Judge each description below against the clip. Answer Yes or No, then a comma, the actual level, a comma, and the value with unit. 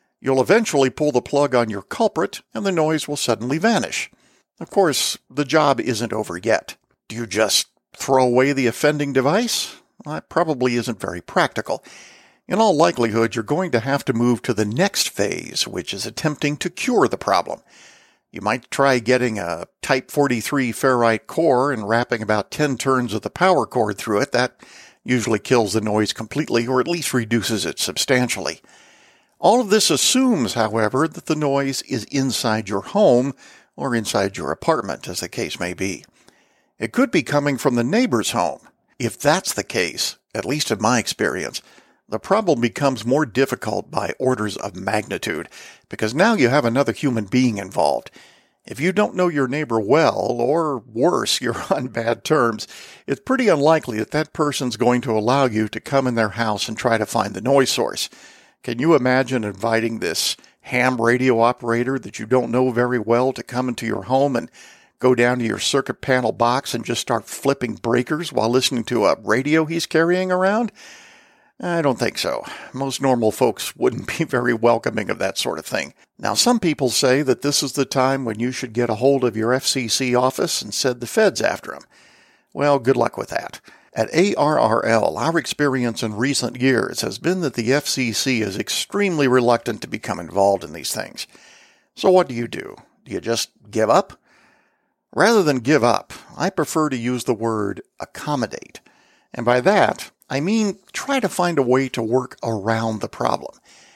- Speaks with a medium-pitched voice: No, low, 125 Hz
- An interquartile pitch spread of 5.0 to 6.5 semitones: No, average, 3.7 semitones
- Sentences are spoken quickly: No, average, 185 wpm